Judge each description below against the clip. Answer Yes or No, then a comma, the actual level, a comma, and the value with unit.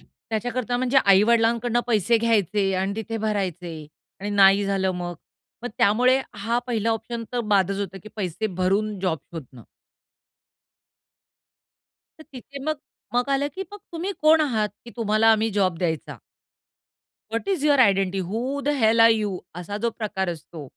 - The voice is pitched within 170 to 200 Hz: No, high, 215 Hz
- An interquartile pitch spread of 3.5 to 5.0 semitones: Yes, average, 3.8 semitones